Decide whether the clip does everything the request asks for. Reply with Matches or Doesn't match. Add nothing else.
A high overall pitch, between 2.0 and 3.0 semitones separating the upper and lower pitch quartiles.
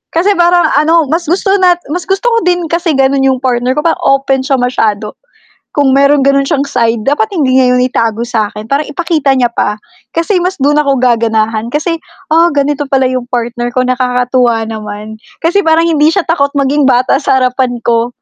Doesn't match